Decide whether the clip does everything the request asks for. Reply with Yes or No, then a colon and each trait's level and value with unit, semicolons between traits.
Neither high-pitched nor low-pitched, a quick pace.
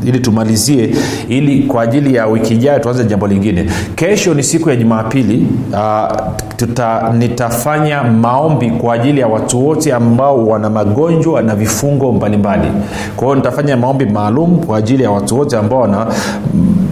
No: low, 120 Hz; fast, 155 wpm